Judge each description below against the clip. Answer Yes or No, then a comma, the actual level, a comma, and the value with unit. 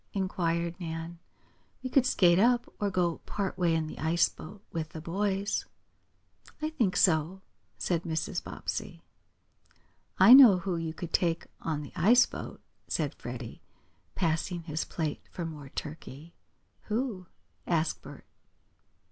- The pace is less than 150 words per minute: Yes, average, 140 wpm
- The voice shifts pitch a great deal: No, average, 3.3 semitones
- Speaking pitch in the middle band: Yes, medium, 170 Hz